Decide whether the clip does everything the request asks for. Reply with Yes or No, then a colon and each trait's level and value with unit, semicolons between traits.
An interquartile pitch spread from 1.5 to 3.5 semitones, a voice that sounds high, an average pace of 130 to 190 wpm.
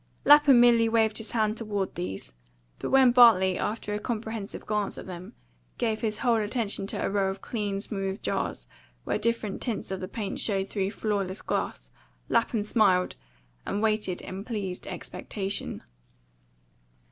Yes: average, 2.8 semitones; high, 210 Hz; average, 155 wpm